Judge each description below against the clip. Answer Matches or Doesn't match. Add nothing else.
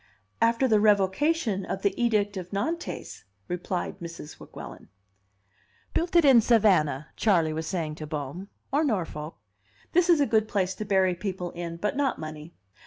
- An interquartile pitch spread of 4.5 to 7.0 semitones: Matches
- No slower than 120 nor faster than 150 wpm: Doesn't match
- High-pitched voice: Matches